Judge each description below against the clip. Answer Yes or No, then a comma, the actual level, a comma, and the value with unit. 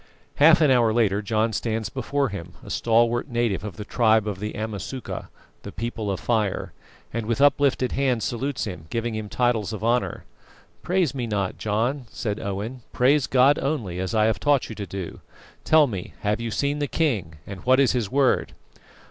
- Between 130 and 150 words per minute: No, average, 190 wpm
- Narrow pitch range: No, average, 3.9 semitones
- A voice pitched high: No, low, 115 Hz